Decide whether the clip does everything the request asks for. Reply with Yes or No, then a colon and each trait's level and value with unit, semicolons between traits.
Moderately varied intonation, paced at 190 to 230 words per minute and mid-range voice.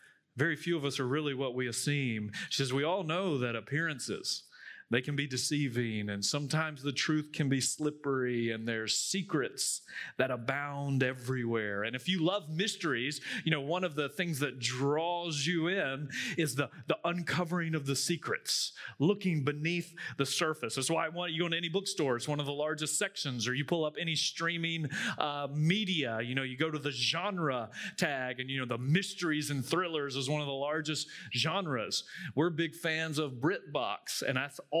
Yes: average, 3.7 semitones; average, 195 wpm; medium, 150 Hz